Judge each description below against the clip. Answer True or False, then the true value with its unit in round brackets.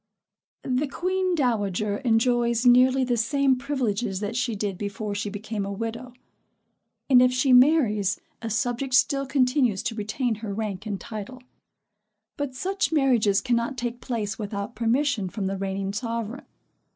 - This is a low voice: False (235 Hz)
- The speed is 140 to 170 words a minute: True (150 wpm)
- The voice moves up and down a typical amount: True (3.6 semitones)